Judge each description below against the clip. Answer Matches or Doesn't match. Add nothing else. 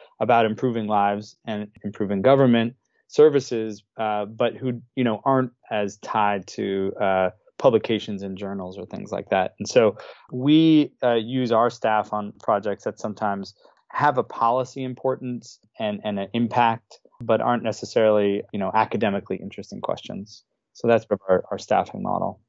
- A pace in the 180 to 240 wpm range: Doesn't match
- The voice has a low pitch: Matches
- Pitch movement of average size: Matches